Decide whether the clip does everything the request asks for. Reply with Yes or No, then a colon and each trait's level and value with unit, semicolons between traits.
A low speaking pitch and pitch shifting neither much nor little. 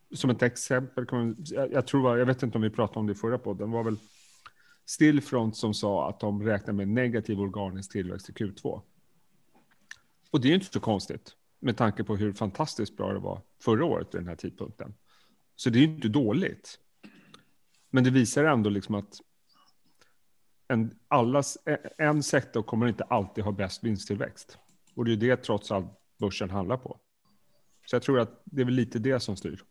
Yes: low, 115 Hz; average, 3.7 semitones